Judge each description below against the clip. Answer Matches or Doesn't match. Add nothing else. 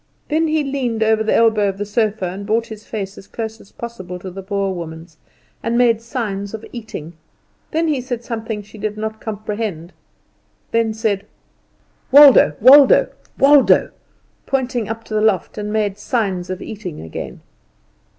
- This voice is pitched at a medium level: Doesn't match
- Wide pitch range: Doesn't match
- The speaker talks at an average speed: Matches